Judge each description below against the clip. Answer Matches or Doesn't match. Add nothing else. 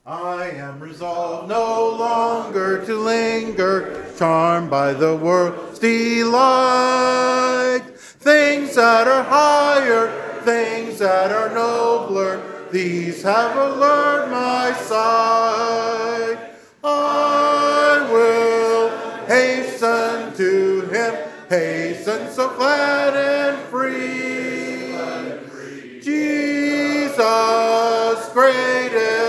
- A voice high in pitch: Matches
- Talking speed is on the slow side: Matches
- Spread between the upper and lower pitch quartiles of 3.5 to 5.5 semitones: Doesn't match